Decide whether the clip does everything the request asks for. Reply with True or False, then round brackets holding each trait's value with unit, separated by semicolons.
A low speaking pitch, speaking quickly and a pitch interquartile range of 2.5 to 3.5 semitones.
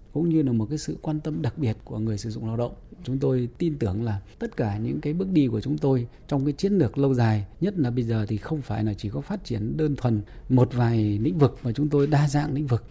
False (130 Hz; 285 wpm; 4.8 semitones)